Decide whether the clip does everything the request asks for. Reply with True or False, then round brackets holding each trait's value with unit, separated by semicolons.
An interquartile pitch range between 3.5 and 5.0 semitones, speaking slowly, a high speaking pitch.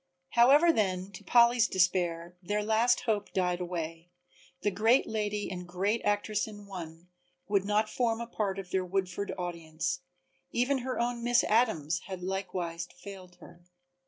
False (3.9 semitones; 160 wpm; 195 Hz)